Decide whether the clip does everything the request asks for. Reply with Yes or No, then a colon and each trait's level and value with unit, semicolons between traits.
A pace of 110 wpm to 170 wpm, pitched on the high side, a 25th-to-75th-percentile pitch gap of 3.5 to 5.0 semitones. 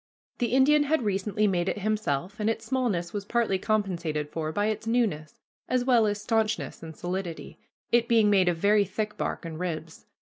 No: average, 190 wpm; high, 205 Hz; average, 4.3 semitones